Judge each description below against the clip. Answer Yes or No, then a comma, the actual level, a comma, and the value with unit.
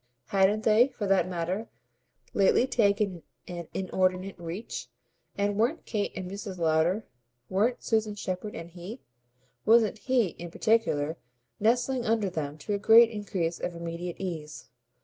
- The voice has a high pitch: Yes, high, 195 Hz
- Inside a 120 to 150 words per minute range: Yes, average, 140 wpm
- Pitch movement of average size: Yes, average, 4.0 semitones